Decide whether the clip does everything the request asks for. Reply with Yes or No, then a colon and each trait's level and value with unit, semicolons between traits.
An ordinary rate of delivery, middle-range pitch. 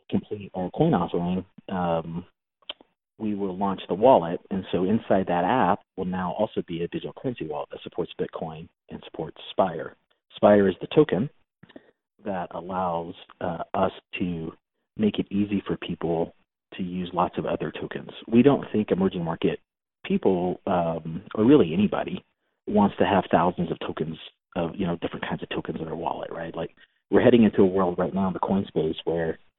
No: average, 180 wpm; very low, 95 Hz